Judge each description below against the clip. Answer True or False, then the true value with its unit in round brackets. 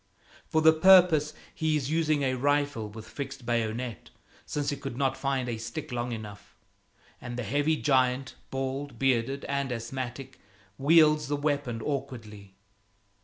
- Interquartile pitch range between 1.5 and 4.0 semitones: True (3.3 semitones)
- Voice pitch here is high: False (135 Hz)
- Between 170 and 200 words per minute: False (145 wpm)